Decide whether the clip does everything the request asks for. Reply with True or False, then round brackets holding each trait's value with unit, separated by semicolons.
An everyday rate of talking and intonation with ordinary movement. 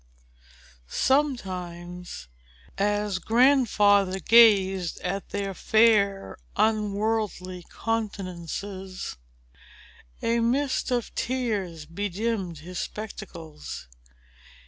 False (65 wpm; 3.7 semitones)